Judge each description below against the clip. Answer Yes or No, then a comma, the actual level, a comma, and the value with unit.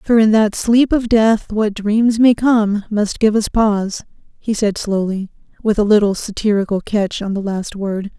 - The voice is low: No, high, 210 Hz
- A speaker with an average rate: Yes, average, 190 wpm